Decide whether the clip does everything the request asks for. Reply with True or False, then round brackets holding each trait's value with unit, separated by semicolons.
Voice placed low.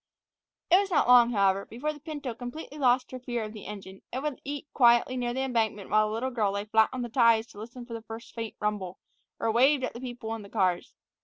False (235 Hz)